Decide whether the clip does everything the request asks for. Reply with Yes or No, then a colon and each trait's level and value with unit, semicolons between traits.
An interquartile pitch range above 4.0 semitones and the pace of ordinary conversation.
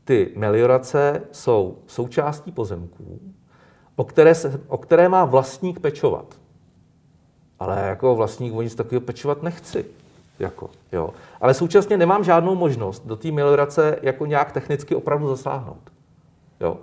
Yes: wide, 5.4 semitones; average, 130 wpm